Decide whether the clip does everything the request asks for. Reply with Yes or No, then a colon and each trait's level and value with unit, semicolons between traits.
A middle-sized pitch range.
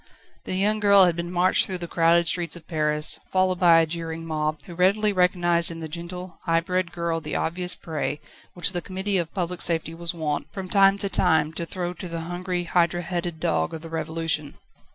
No: narrow, 1.9 semitones